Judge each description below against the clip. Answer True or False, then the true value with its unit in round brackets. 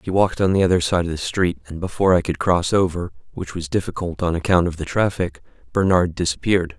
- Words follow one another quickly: True (220 wpm)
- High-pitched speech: False (90 Hz)